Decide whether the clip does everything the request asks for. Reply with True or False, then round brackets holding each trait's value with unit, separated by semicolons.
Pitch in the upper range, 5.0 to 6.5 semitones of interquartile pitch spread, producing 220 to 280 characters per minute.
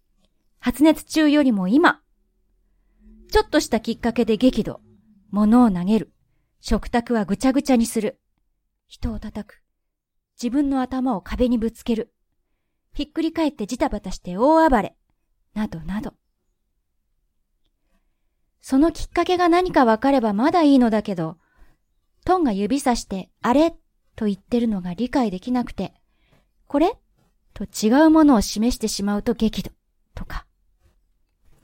True (230 Hz; 5.5 semitones; 255 characters per minute)